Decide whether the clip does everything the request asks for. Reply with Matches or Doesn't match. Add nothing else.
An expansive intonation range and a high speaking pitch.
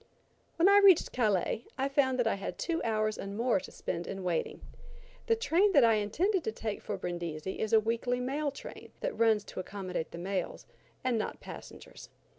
Matches